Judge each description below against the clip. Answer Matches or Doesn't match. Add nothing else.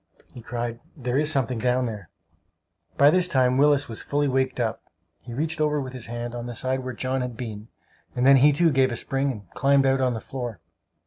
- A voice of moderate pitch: Doesn't match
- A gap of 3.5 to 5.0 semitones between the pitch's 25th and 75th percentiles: Doesn't match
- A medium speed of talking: Doesn't match